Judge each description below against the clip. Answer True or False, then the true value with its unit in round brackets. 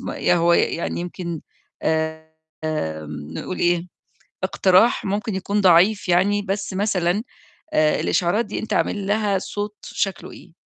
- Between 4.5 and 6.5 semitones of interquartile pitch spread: False (3.1 semitones)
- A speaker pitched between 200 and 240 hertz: False (190 Hz)